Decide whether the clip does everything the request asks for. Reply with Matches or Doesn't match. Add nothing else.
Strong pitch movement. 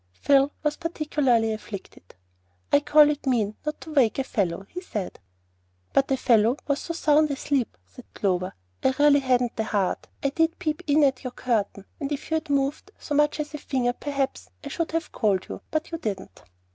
Doesn't match